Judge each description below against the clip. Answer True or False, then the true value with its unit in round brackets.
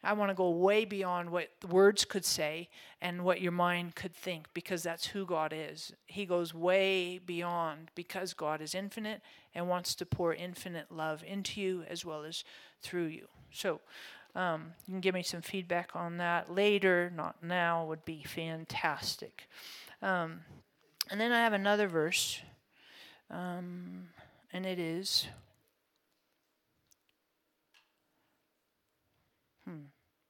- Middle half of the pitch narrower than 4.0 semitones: True (2.4 semitones)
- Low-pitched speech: False (175 Hz)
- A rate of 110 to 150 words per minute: True (140 wpm)